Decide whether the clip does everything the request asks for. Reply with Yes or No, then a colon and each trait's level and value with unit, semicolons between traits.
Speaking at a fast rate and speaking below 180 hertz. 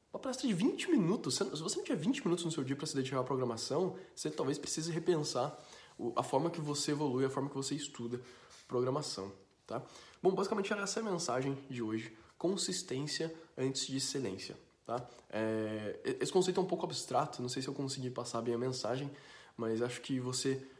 Yes: fast, 200 wpm; low, 135 Hz